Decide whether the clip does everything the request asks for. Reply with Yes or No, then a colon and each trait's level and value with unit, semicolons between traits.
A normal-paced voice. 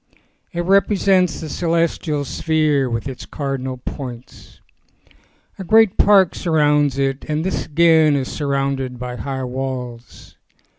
No: slow, 120 wpm